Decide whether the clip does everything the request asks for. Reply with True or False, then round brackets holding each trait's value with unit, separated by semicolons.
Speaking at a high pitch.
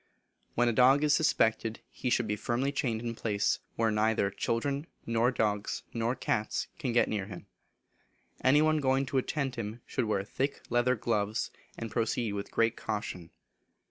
False (115 Hz)